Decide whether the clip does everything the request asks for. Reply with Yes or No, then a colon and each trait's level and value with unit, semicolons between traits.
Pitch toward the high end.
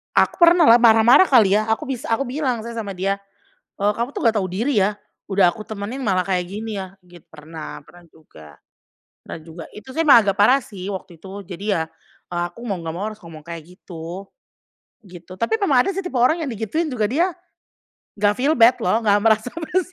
Yes: high, 210 Hz